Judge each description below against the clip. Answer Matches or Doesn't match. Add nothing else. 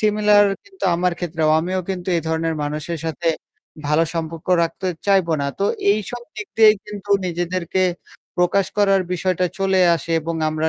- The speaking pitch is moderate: Matches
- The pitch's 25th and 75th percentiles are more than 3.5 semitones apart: Doesn't match